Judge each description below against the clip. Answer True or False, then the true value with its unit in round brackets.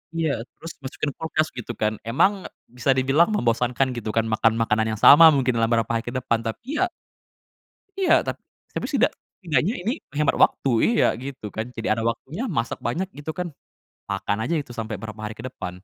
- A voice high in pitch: False (125 Hz)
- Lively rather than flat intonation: True (5.8 semitones)